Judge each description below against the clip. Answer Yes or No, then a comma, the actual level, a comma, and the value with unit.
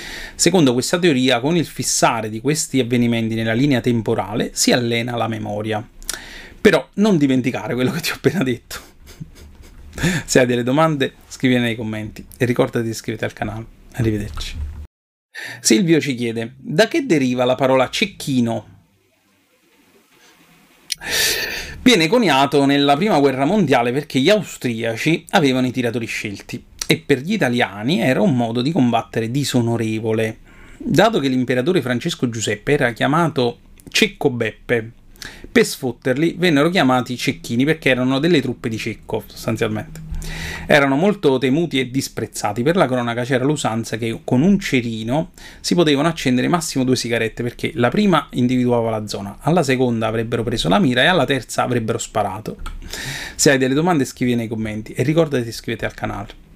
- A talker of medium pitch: No, low, 125 Hz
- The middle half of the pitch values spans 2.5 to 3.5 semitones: No, average, 3.9 semitones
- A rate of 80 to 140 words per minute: No, average, 150 wpm